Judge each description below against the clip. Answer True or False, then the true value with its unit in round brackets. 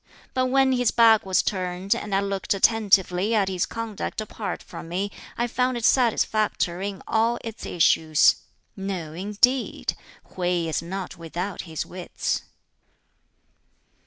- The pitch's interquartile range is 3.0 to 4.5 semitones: True (3.9 semitones)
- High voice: True (195 Hz)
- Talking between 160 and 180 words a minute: False (135 wpm)